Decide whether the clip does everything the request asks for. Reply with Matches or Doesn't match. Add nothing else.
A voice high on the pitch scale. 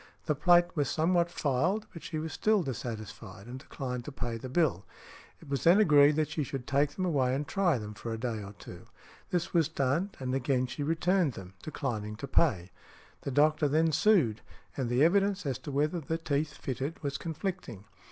Doesn't match